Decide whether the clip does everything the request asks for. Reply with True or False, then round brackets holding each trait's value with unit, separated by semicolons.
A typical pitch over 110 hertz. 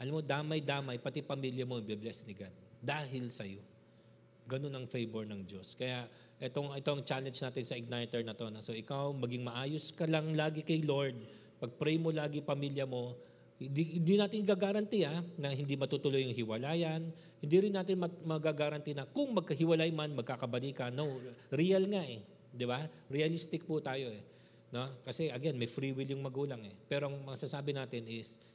True (140 Hz)